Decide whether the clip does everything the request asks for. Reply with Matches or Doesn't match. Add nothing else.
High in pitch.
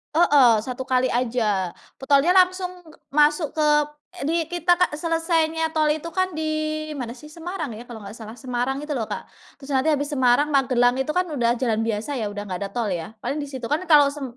Matches